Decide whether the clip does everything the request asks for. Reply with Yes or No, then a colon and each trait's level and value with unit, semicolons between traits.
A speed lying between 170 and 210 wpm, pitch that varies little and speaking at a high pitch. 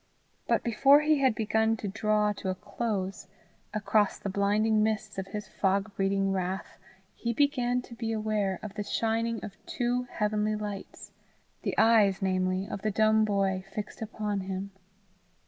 No: average, 160 wpm; narrow, 2.3 semitones; high, 210 Hz